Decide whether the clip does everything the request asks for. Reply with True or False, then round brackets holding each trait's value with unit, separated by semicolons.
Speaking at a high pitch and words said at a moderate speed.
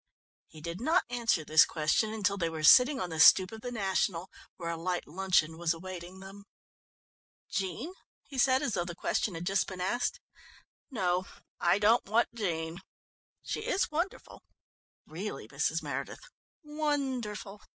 True (195 Hz; 155 wpm)